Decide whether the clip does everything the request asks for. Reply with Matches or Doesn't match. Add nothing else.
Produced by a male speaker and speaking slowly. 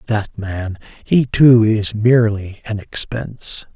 Matches